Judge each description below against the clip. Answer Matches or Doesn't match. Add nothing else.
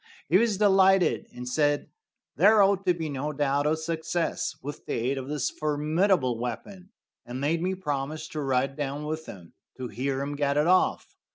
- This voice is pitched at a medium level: Matches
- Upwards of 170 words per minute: Matches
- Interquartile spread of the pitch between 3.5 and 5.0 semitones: Matches